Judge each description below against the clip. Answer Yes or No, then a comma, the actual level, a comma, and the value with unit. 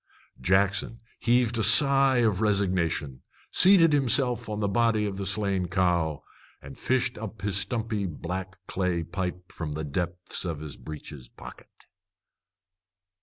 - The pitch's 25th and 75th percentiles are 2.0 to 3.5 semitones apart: No, average, 4.8 semitones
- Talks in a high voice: No, low, 100 Hz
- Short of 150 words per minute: Yes, slow, 135 wpm